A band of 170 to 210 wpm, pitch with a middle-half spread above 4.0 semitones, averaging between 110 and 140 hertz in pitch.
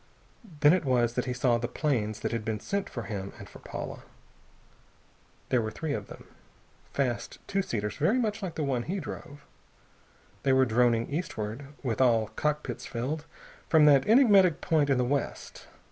Yes: average, 175 wpm; average, 5.1 semitones; low, 135 Hz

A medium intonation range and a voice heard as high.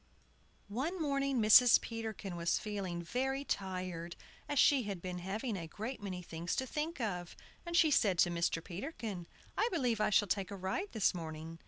No: wide, 6.8 semitones; high, 205 Hz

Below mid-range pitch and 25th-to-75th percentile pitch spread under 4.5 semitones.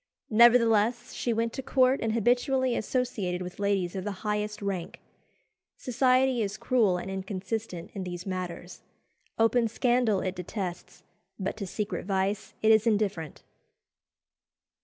No: high, 210 Hz; average, 3.9 semitones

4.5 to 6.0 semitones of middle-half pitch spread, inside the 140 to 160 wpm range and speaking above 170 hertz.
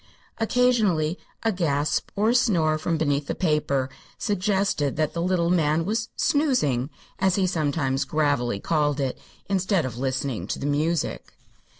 No: average, 5.1 semitones; average, 150 wpm; medium, 160 Hz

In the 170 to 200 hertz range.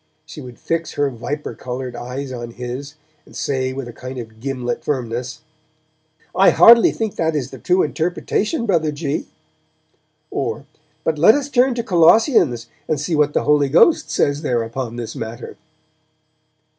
No: medium, 140 Hz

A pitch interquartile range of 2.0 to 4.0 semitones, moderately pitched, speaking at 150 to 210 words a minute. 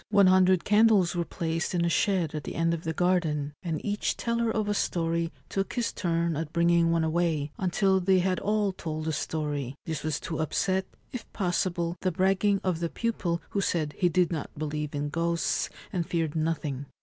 Yes: average, 2.9 semitones; medium, 170 Hz; average, 195 wpm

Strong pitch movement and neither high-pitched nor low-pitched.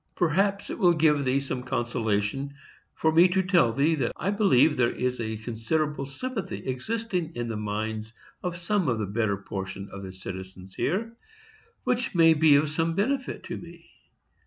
Yes: wide, 7.7 semitones; medium, 145 Hz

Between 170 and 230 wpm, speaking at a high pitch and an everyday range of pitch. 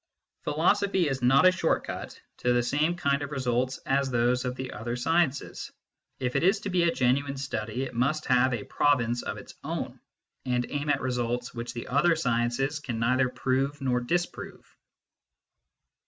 No: average, 175 wpm; low, 130 Hz; average, 3.1 semitones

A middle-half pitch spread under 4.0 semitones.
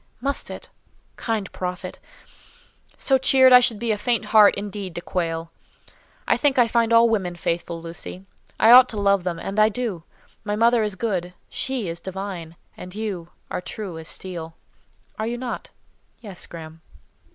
No: average, 4.6 semitones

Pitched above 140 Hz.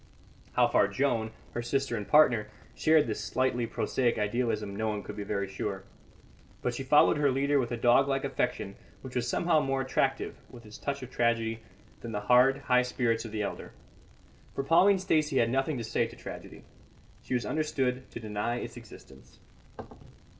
No: low, 120 Hz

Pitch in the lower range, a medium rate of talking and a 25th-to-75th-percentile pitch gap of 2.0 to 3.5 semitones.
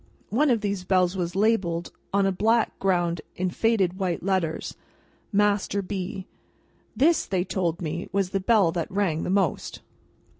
No: high, 190 Hz; average, 155 wpm; narrow, 2.5 semitones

